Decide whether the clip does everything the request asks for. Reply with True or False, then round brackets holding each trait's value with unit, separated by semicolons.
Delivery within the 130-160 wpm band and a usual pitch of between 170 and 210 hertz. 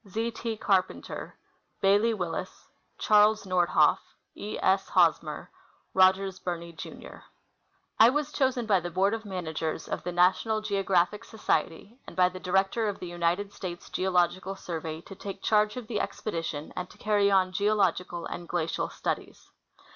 True (155 wpm; 190 Hz)